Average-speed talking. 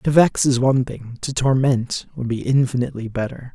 Yes: average, 185 wpm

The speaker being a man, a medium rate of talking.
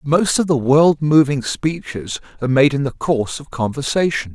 Yes: male; average, 180 wpm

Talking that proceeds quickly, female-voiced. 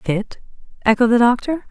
No: average, 140 wpm; female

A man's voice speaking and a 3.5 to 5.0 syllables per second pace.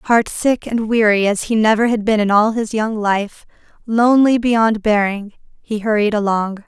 No: female; 4.5 syllables/s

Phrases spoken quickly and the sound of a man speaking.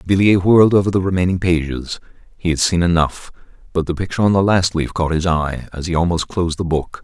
Yes: fast, 220 wpm; male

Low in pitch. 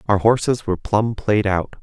Yes: low, 105 Hz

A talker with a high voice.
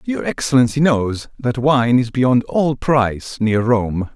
No: low, 125 Hz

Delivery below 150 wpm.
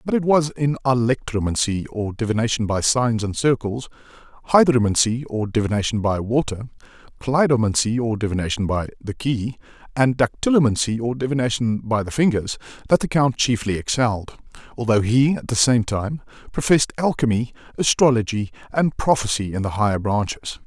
Yes: average, 140 wpm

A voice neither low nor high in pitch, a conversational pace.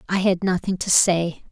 Yes: medium, 180 Hz; average, 195 wpm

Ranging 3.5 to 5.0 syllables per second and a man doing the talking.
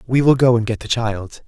No: 5.3 syllables/s; male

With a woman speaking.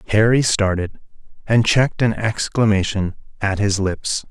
No: male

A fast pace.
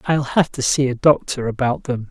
Yes: fast, 230 wpm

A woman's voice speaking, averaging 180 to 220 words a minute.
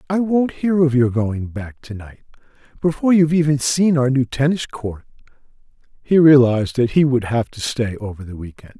No: male; average, 190 wpm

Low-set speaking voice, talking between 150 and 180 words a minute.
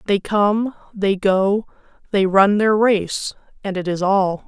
No: high, 200 Hz; average, 160 wpm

